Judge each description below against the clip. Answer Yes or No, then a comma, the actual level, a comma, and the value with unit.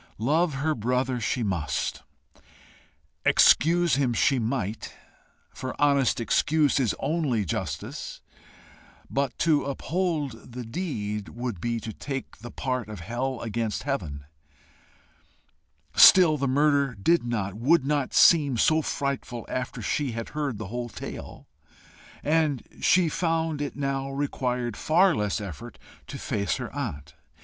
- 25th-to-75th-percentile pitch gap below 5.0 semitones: Yes, average, 4.5 semitones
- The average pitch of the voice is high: No, low, 130 Hz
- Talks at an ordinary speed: No, slow, 130 wpm